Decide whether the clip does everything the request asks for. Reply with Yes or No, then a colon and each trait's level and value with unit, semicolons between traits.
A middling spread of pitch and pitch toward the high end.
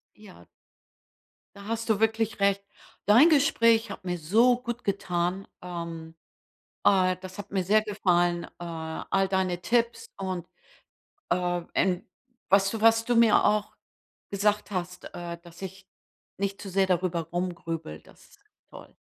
Yes: average, 3.2 semitones; high, 195 Hz